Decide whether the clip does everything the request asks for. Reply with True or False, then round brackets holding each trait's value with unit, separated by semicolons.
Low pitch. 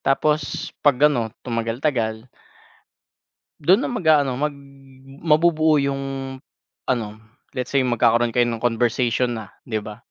True (125 Hz)